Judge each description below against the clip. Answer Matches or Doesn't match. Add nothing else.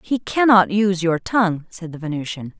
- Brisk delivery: Doesn't match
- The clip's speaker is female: Matches